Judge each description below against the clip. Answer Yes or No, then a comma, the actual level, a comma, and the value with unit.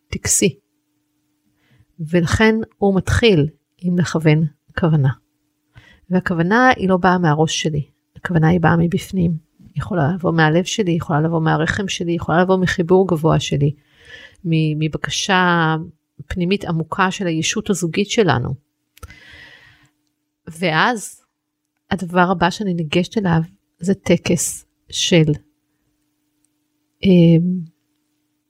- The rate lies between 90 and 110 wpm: Yes, slow, 100 wpm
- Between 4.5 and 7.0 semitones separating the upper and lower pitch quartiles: No, average, 3.2 semitones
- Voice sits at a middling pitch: Yes, medium, 160 Hz